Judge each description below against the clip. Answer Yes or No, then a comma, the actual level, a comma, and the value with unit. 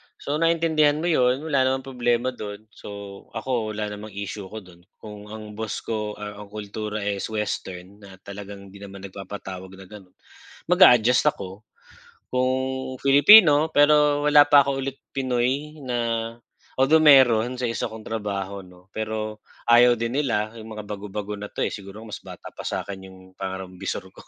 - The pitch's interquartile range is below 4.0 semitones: No, average, 4.6 semitones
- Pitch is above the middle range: No, low, 110 Hz